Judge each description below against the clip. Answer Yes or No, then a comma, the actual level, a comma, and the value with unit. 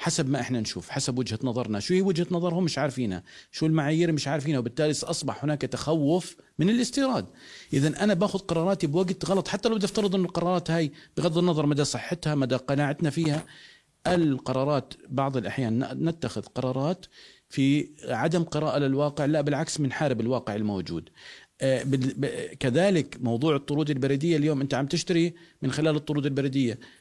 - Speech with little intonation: No, average, 4.3 semitones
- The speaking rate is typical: No, fast, 155 wpm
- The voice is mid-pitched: Yes, medium, 150 Hz